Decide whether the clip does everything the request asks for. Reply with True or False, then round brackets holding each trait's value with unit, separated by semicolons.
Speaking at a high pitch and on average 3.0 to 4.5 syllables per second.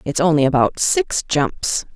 False (165 Hz; 3.9 syllables/s)